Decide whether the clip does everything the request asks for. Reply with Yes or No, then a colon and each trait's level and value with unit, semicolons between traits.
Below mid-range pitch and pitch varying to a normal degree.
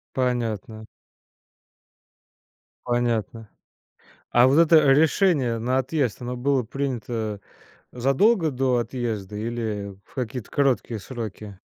Yes: low, 120 Hz; average, 3.4 semitones